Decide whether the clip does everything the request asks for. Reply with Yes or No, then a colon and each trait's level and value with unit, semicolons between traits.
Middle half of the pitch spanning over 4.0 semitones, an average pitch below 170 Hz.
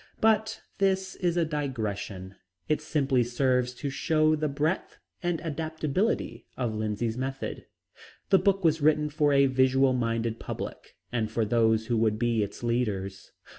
Yes: average, 5.3 semitones; low, 135 Hz